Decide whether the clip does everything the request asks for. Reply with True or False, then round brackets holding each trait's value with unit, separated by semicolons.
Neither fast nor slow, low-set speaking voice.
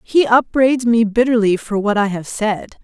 False (190 wpm; 225 Hz)